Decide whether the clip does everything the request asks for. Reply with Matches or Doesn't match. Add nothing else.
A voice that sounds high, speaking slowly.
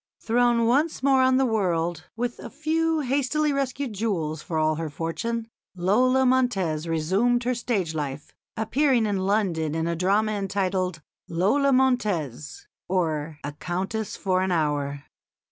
Doesn't match